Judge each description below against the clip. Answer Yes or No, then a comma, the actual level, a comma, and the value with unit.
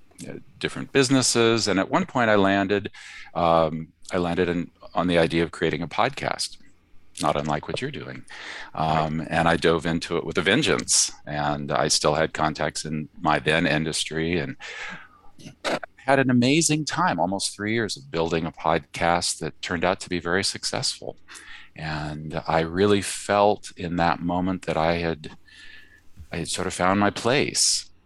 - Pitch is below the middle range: Yes, very low, 85 Hz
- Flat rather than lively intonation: No, average, 3.6 semitones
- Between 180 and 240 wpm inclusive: No, average, 165 wpm